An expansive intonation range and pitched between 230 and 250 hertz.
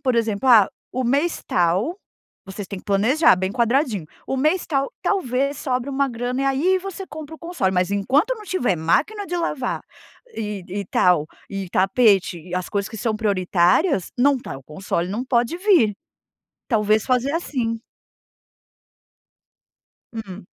Yes: wide, 6.4 semitones; high, 235 Hz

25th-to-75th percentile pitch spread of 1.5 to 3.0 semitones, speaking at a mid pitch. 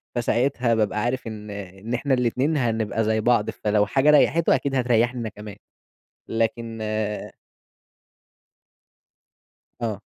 No: average, 2.7 semitones; low, 115 Hz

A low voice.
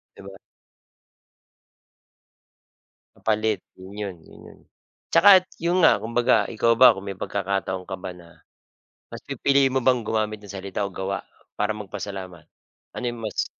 Yes: low, 105 Hz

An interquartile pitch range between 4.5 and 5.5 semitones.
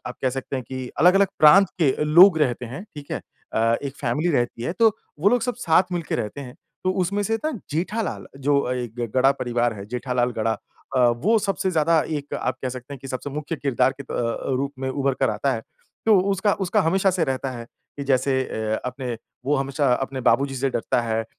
Yes: average, 5.0 semitones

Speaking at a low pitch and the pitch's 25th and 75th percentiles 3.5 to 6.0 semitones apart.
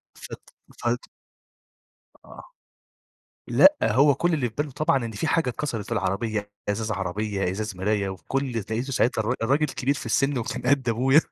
Yes: low, 120 Hz; average, 4.6 semitones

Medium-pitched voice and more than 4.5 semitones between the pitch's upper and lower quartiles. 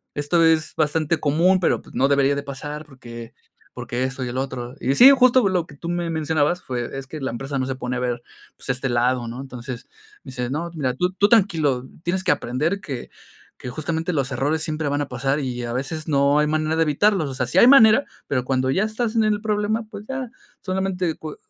Yes: medium, 150 Hz; average, 5.3 semitones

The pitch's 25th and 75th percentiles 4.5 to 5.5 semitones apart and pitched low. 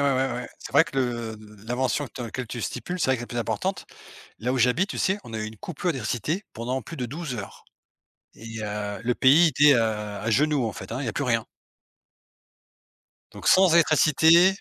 Yes: average, 5.0 semitones; low, 125 Hz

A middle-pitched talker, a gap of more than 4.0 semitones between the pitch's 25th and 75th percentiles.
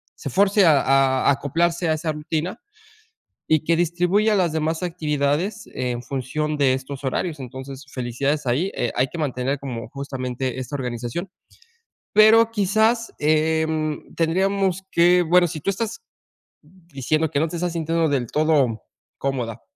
Yes: medium, 155 Hz; average, 4.5 semitones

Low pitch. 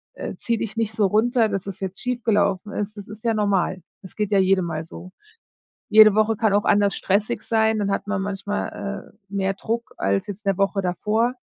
No: high, 205 Hz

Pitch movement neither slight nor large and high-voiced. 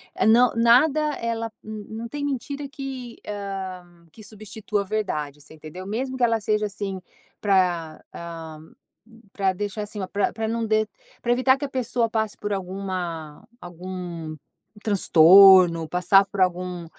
Yes: average, 4.1 semitones; high, 200 Hz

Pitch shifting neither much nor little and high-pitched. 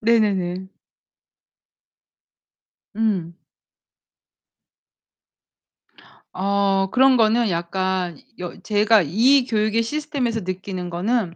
Yes: average, 3.8 semitones; high, 205 Hz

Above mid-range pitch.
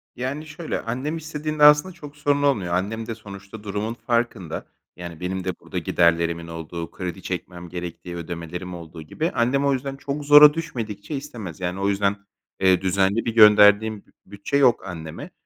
No: low, 105 Hz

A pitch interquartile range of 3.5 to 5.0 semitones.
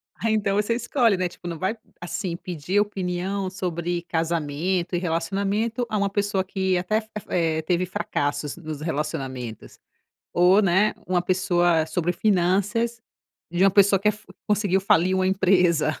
No: average, 2.8 semitones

